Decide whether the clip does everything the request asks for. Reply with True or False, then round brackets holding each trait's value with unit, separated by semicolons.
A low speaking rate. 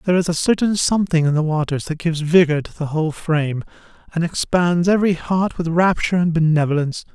False (195 wpm)